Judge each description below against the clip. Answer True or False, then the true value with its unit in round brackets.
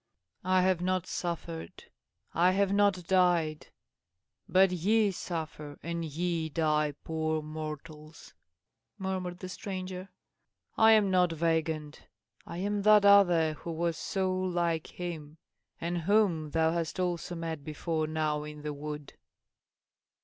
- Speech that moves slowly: True (130 wpm)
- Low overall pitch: False (170 Hz)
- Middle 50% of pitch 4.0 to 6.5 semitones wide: False (2.9 semitones)